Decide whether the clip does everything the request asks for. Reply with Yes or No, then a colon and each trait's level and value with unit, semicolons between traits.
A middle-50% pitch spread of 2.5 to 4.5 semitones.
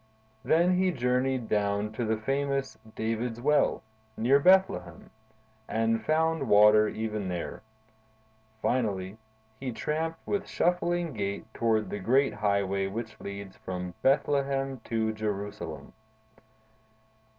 No: average, 5.1 semitones